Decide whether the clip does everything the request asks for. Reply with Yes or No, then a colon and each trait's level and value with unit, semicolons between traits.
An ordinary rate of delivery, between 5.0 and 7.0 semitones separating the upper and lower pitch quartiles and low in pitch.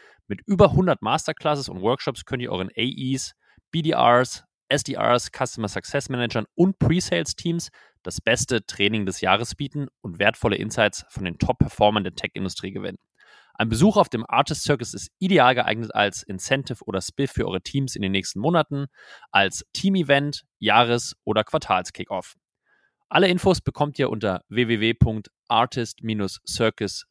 Yes: average, 150 wpm; wide, 5.6 semitones; low, 125 Hz